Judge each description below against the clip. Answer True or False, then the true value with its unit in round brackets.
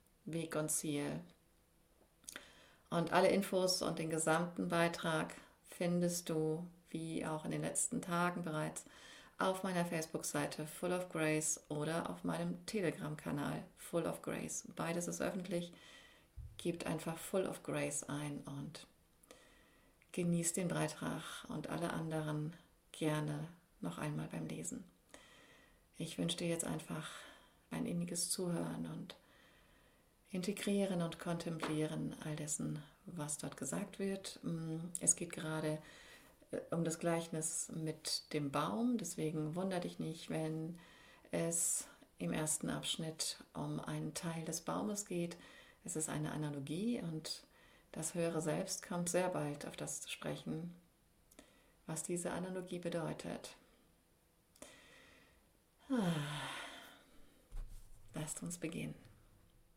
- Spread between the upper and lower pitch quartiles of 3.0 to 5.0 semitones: False (2.4 semitones)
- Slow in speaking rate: True (115 wpm)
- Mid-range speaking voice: True (160 Hz)